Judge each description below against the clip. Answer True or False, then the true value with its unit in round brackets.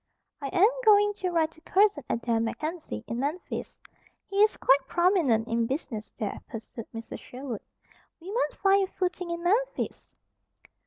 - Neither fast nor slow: True (155 wpm)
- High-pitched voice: True (325 Hz)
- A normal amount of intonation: False (8.5 semitones)